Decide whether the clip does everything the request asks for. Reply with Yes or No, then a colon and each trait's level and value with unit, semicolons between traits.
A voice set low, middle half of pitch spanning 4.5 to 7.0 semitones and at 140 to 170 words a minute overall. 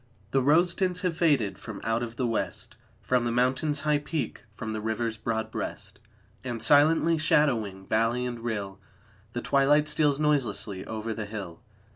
Yes: low, 120 Hz; average, 5.0 semitones; average, 165 wpm